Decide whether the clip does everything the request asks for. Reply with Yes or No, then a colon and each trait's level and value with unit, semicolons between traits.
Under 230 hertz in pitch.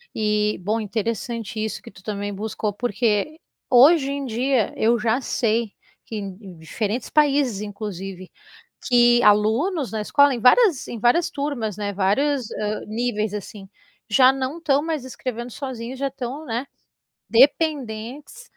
No: high, 235 Hz